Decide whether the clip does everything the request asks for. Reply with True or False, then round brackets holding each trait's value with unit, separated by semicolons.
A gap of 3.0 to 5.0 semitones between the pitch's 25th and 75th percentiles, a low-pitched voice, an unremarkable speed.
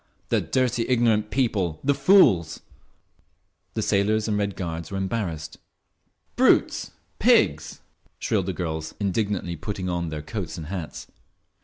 False (4.4 semitones; 95 Hz; 130 wpm)